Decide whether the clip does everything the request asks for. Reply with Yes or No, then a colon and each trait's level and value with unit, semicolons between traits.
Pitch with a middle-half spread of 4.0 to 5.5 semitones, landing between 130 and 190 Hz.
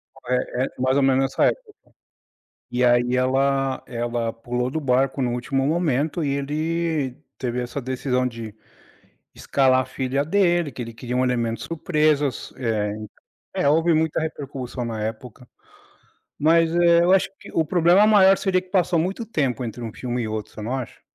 Yes: average, 4.7 semitones; low, 135 Hz